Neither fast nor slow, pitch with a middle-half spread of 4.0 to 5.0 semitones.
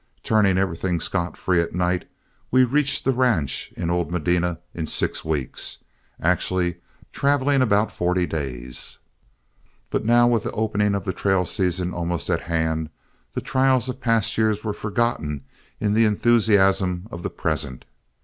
Yes: average, 150 wpm; average, 4.5 semitones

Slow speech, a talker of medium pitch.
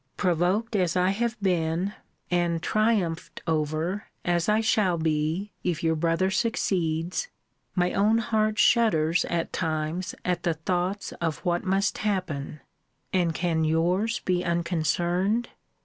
Yes: slow, 130 wpm; medium, 175 Hz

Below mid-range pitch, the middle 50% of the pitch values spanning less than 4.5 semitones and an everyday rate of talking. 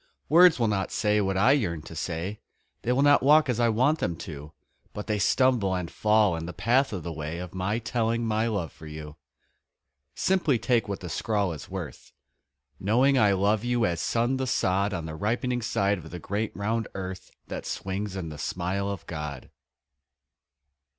No: low, 100 Hz; average, 4.9 semitones; average, 190 wpm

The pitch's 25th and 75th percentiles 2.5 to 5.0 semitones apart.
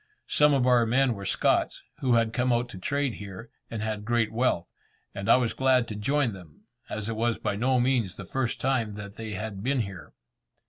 Yes: average, 3.7 semitones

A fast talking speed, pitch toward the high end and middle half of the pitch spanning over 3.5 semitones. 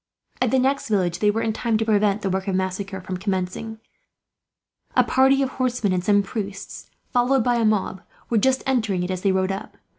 Yes: fast, 210 wpm; high, 210 Hz; average, 4.2 semitones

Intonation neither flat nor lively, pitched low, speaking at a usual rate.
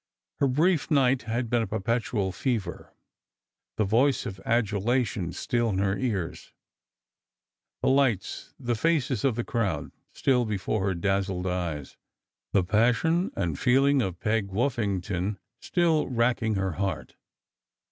No: average, 4.7 semitones; low, 110 Hz; slow, 130 wpm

